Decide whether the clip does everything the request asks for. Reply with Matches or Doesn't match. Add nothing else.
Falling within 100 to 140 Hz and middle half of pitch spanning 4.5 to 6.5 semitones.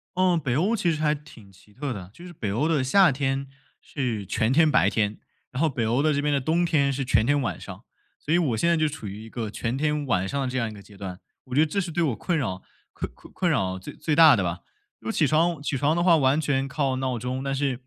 Matches